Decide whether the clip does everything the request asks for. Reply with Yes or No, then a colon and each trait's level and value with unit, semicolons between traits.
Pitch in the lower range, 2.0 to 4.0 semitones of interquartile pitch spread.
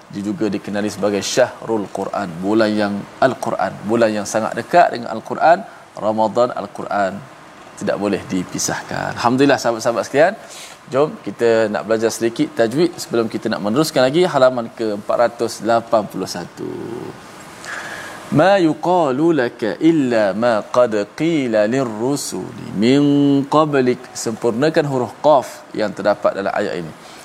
No: low, 115 Hz; average, 4.6 semitones